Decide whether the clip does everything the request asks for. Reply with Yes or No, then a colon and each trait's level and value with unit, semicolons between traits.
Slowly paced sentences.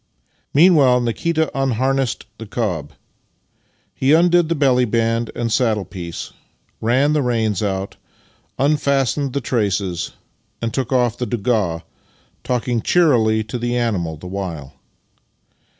Yes: slow, 120 wpm